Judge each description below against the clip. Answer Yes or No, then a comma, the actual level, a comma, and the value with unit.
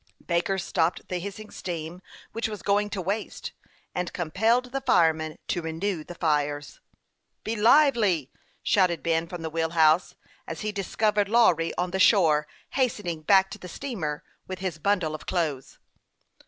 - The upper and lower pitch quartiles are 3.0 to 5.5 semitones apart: Yes, average, 4.2 semitones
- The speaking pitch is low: No, medium, 180 Hz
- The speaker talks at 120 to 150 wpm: No, average, 165 wpm